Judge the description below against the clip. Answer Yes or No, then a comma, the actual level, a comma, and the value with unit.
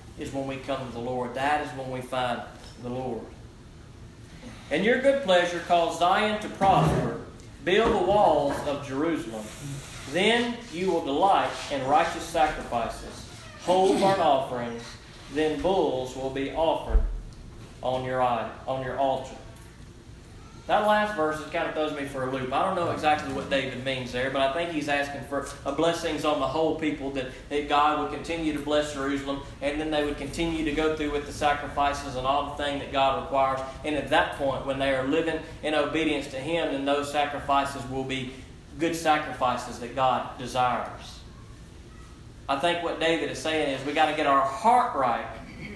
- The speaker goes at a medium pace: Yes, average, 180 wpm